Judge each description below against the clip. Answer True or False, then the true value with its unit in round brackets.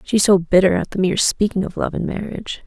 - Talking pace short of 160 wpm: False (250 wpm)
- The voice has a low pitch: False (195 Hz)